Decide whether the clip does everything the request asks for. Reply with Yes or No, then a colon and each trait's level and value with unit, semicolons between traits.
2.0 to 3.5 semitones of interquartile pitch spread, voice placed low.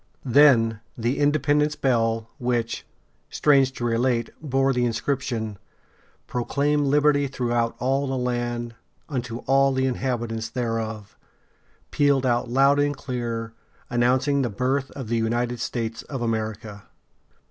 Yes: average, 3.0 semitones; low, 125 Hz